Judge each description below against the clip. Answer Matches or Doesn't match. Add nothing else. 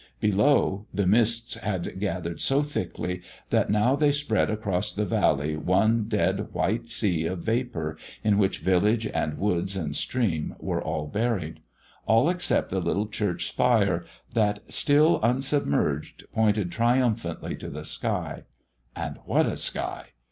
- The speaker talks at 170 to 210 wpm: Doesn't match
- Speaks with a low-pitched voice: Matches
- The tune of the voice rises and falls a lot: Doesn't match